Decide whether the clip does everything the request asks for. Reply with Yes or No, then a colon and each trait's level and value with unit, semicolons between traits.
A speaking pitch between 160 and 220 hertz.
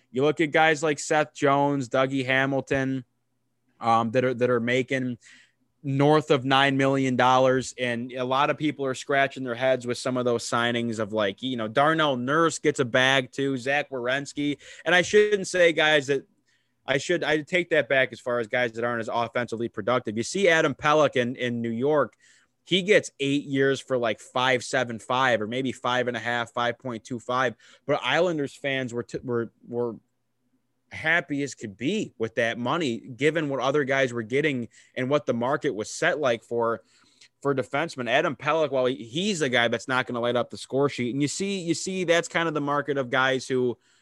No: low, 130 Hz